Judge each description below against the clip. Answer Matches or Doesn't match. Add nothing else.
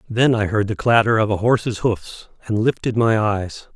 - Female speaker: Doesn't match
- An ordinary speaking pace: Doesn't match